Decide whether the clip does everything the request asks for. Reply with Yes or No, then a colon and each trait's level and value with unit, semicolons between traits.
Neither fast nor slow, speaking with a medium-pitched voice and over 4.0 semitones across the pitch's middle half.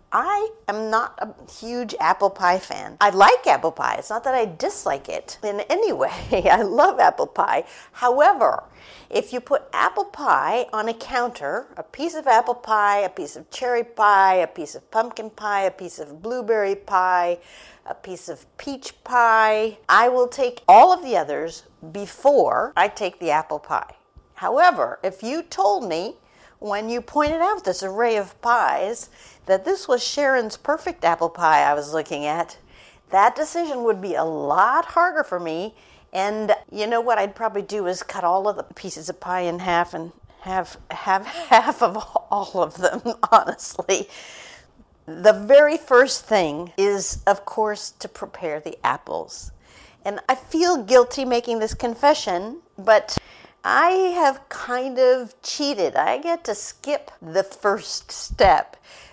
No: average, 165 wpm; high, 220 Hz; average, 5.3 semitones